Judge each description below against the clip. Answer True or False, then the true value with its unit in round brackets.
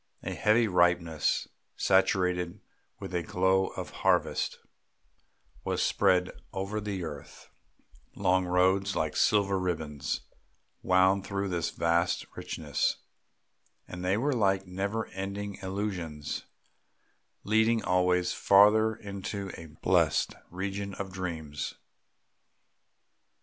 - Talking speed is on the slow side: True (100 wpm)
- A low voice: True (95 Hz)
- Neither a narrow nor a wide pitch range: False (2.0 semitones)